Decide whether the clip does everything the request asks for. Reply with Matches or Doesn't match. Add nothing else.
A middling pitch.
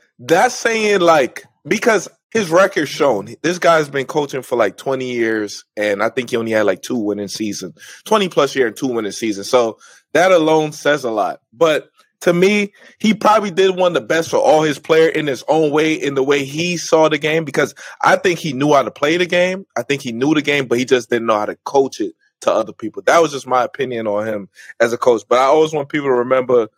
Matches